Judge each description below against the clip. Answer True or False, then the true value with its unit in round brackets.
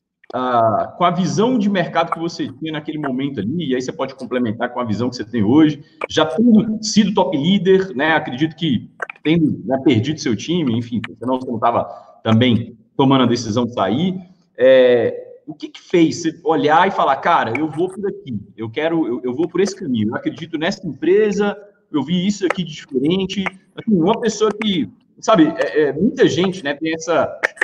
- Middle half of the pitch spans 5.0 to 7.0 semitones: True (5.6 semitones)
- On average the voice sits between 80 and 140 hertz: False (170 Hz)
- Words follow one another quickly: True (200 wpm)